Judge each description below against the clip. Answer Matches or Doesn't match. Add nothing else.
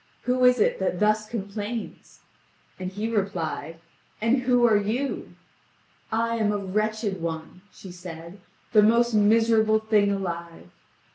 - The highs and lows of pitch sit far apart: Doesn't match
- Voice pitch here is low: Doesn't match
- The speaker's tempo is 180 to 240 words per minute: Doesn't match